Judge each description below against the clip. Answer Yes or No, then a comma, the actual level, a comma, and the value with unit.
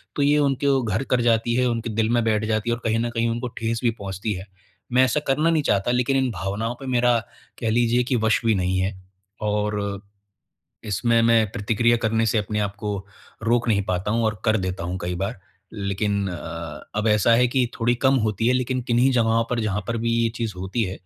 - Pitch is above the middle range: No, low, 115 Hz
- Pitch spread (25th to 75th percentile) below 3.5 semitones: Yes, narrow, 2.6 semitones